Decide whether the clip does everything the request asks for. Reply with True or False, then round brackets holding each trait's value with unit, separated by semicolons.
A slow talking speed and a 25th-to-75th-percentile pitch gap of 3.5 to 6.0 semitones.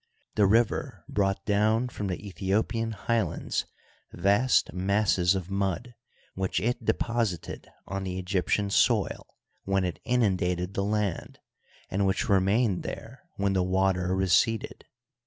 False (130 wpm; 2.4 semitones)